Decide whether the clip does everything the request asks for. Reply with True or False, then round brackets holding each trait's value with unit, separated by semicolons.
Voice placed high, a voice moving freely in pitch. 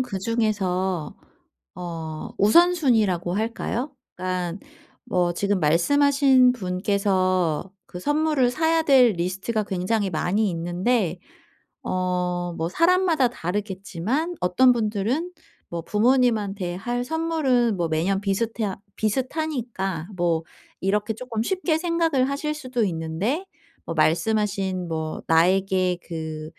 True (205 Hz; 6.0 semitones)